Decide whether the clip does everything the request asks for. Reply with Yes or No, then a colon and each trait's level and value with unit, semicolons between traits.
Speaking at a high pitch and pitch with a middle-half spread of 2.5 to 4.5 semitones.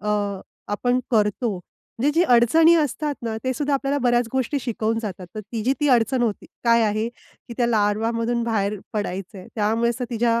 Yes: high, 235 Hz; average, 2.8 semitones